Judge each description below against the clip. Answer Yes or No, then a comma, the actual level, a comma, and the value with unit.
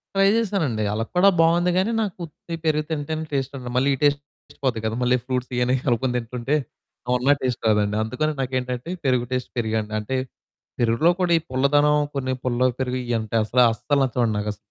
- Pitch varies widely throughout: No, average, 3.7 semitones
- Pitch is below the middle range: Yes, low, 130 Hz